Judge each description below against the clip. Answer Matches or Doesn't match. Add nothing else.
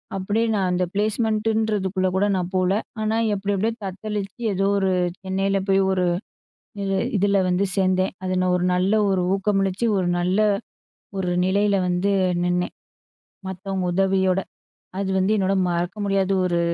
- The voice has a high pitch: Matches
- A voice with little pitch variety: Matches